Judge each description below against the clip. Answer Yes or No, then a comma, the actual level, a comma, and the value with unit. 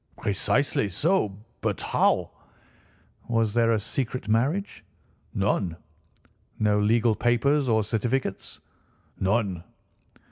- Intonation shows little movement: No, average, 3.5 semitones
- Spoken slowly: Yes, slow, 95 wpm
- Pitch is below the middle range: Yes, low, 115 Hz